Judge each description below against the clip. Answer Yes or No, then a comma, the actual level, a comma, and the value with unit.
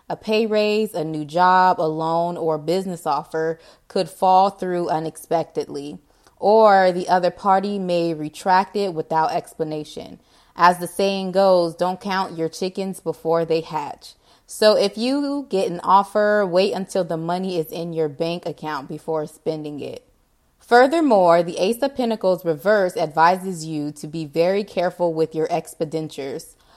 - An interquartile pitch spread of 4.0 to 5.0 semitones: No, average, 3.2 semitones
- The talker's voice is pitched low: No, medium, 175 Hz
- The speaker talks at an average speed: Yes, average, 155 wpm